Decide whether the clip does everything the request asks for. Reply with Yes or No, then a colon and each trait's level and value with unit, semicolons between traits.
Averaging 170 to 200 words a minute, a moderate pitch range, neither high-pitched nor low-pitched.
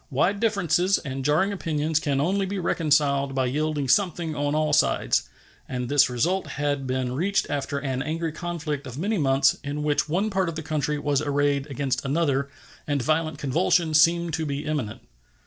Yes: average, 180 wpm; average, 3.1 semitones; medium, 150 Hz